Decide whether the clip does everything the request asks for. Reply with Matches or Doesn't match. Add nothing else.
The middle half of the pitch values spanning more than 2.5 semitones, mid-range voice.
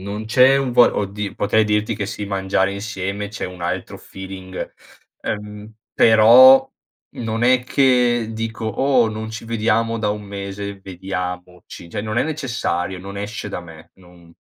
Doesn't match